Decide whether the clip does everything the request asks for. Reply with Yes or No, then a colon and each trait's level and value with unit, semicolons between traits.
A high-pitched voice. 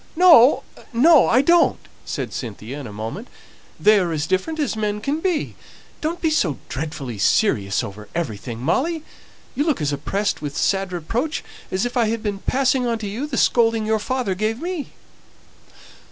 Yes: high, 215 Hz